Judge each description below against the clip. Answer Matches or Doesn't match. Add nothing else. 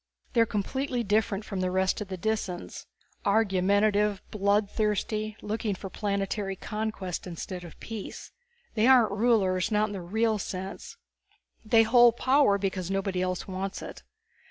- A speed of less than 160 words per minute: Matches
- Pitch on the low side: Doesn't match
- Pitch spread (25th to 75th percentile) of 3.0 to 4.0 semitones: Doesn't match